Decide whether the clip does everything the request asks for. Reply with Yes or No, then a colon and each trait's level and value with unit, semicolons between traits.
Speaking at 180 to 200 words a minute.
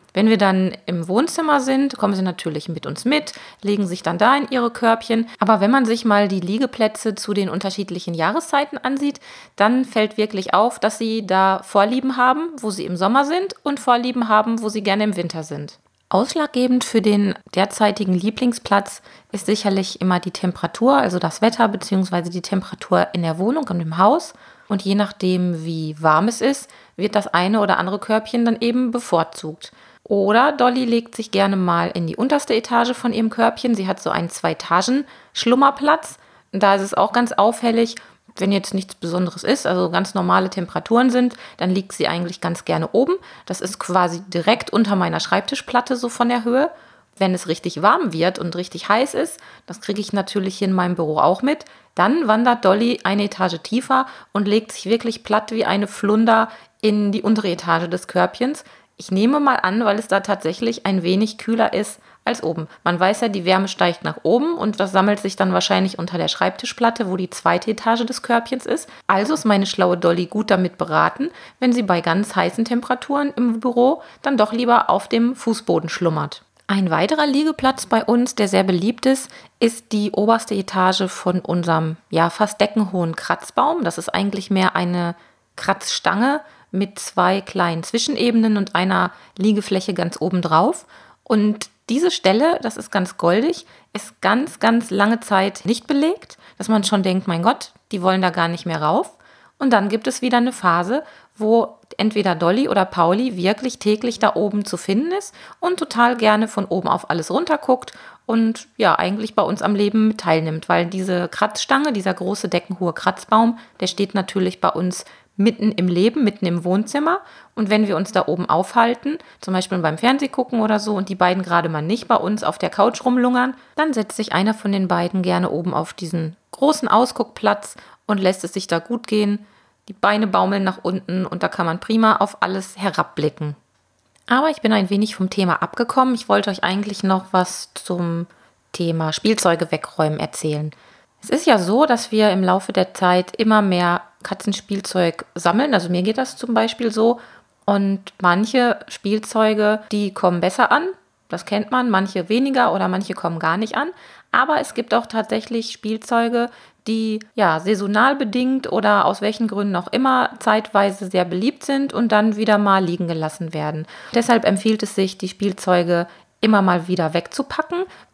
Yes: average, 185 wpm